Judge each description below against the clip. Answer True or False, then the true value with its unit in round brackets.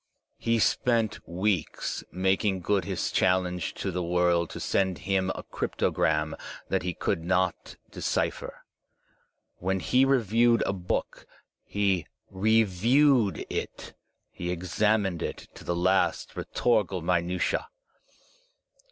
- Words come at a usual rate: False (115 wpm)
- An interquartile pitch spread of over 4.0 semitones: False (3.4 semitones)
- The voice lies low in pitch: True (95 Hz)